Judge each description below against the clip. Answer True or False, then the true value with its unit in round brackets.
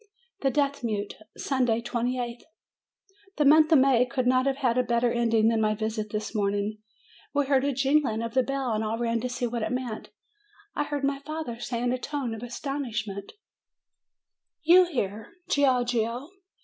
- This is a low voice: False (245 Hz)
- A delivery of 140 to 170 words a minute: False (180 wpm)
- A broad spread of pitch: False (3.4 semitones)